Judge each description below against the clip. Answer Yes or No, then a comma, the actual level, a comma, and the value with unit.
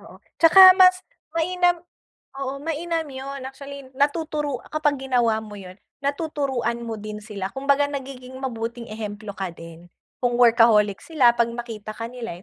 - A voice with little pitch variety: No, average, 4.6 semitones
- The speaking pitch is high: Yes, very high, 260 Hz